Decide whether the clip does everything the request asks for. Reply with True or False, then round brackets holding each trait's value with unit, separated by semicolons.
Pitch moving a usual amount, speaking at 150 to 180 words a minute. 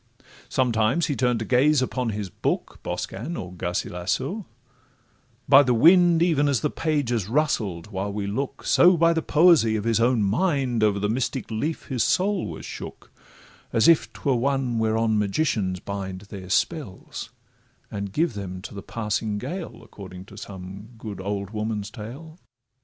False (5.9 semitones; 160 wpm)